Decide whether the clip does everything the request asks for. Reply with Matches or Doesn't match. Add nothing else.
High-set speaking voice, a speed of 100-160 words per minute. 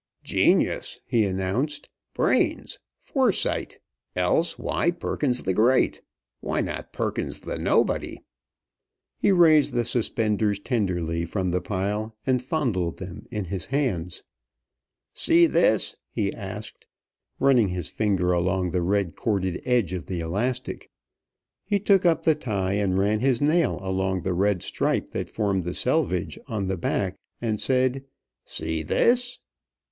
Doesn't match